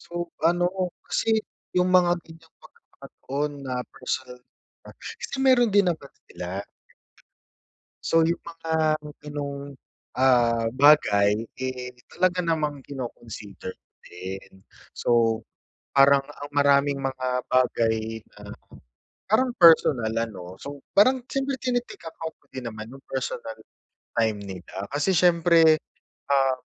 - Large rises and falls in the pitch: Yes, wide, 6.1 semitones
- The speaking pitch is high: No, medium, 140 Hz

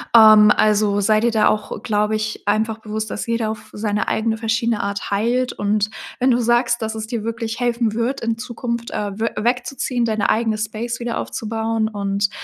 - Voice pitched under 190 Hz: No, high, 220 Hz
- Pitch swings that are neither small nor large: No, narrow, 1.7 semitones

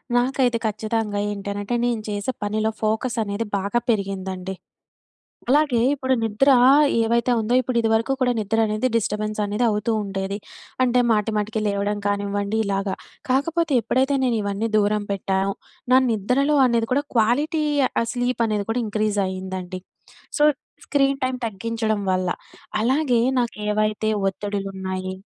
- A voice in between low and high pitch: No, high, 215 Hz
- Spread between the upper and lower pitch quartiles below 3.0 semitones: No, average, 3.3 semitones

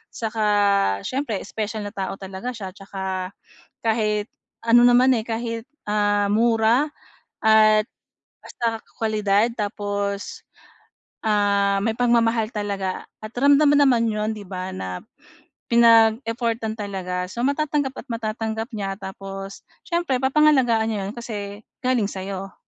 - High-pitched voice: Yes, high, 215 Hz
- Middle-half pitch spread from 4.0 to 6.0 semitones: No, average, 2.7 semitones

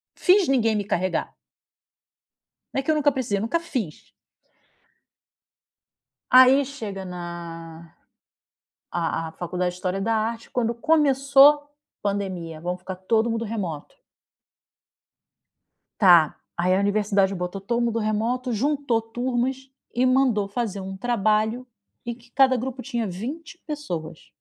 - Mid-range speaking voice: No, high, 225 Hz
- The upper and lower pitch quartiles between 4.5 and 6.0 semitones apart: Yes, wide, 5.5 semitones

